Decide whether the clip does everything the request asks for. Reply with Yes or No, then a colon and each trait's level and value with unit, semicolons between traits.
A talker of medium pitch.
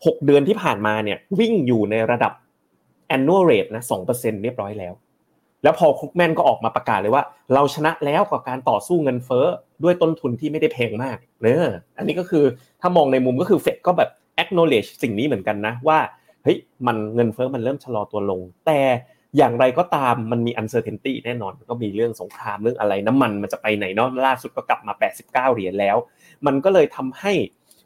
No: low, 125 Hz